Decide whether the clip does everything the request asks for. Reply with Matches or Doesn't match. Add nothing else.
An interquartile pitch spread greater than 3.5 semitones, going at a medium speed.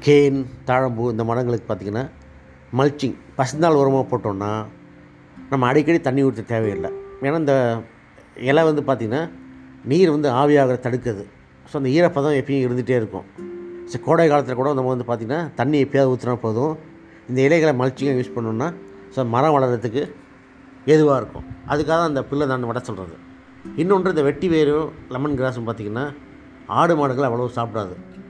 Doesn't match